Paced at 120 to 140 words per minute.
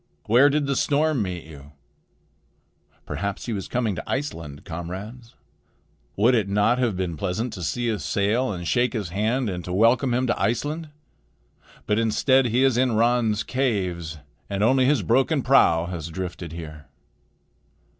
No: average, 165 wpm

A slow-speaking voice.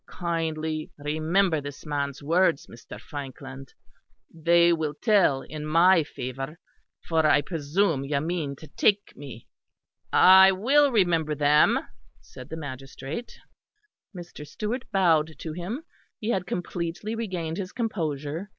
Yes: slow, 125 wpm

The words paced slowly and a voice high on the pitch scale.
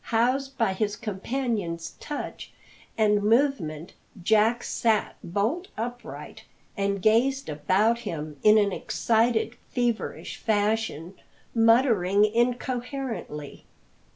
Yes: slow, 95 wpm; high, 220 Hz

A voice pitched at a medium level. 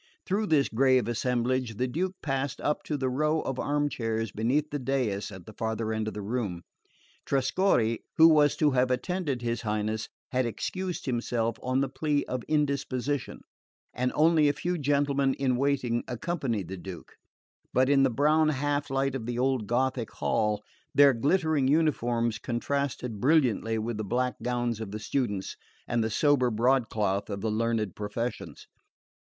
No: low, 125 Hz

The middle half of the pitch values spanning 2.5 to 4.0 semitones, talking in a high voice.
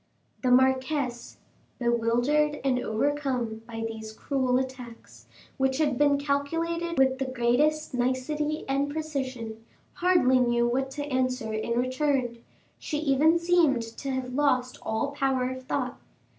Yes: average, 2.9 semitones; very high, 260 Hz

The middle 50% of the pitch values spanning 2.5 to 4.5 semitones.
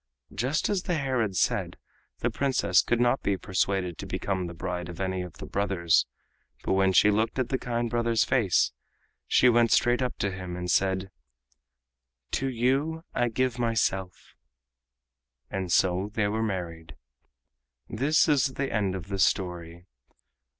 No: average, 4.9 semitones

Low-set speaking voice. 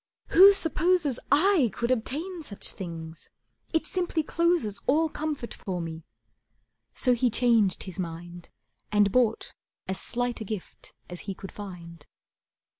No: high, 235 Hz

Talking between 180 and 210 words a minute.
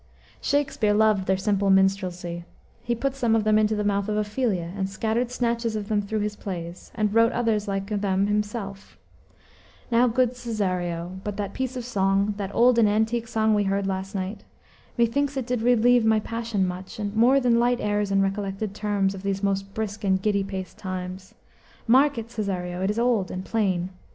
Yes: average, 190 wpm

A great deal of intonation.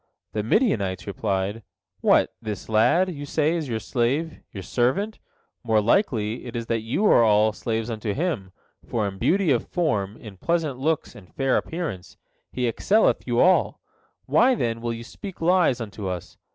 Yes: wide, 7.2 semitones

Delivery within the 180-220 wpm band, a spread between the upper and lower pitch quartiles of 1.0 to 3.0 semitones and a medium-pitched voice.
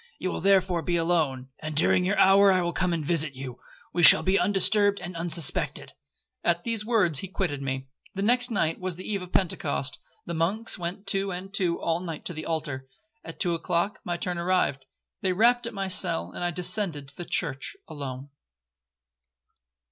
No: average, 185 wpm; average, 3.7 semitones; medium, 175 Hz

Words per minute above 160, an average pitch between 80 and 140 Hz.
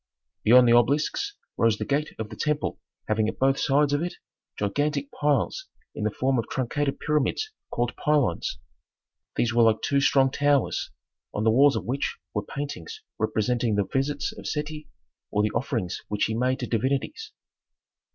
Yes: average, 170 wpm; low, 135 Hz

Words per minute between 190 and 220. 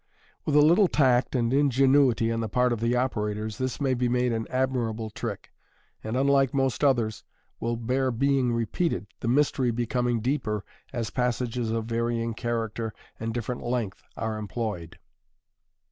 No: average, 155 wpm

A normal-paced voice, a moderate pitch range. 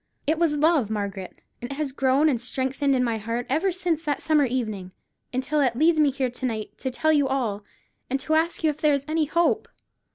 No: fast, 225 wpm; average, 4.1 semitones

